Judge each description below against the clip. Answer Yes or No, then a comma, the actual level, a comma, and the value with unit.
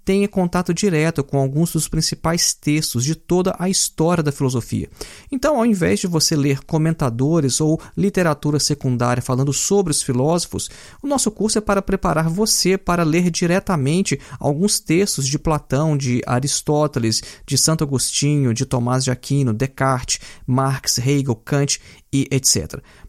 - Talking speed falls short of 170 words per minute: Yes, average, 150 wpm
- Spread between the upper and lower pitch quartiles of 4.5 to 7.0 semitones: Yes, average, 4.8 semitones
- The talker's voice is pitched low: No, medium, 150 Hz